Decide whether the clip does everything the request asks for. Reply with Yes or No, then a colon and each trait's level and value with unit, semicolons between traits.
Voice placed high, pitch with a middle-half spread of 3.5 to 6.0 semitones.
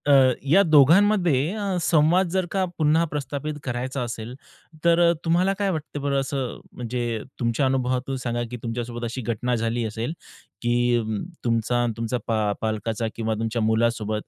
No: low, 125 Hz; average, 4.8 semitones